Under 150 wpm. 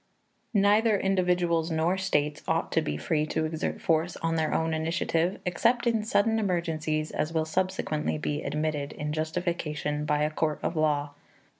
No: average, 165 wpm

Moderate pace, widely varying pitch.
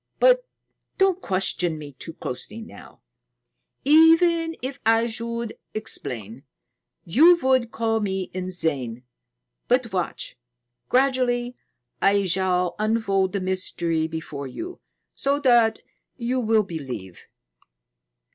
No: slow, 105 wpm; wide, 6.7 semitones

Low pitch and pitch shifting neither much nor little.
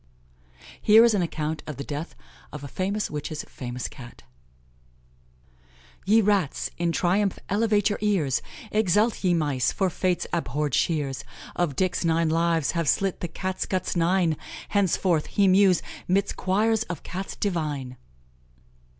No: medium, 175 Hz; average, 4.5 semitones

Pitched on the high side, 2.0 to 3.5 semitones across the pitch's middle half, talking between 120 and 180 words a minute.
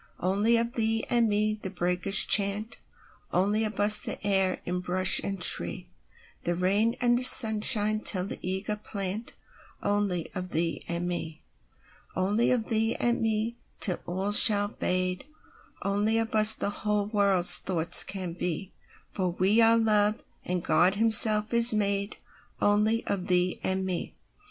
Yes: high, 205 Hz; average, 3.0 semitones; slow, 135 wpm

